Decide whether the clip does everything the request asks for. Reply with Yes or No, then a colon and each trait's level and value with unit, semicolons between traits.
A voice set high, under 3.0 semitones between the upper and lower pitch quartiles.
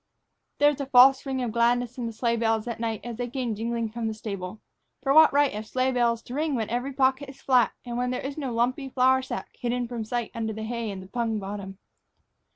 Yes: high, 240 Hz; narrow, 2.6 semitones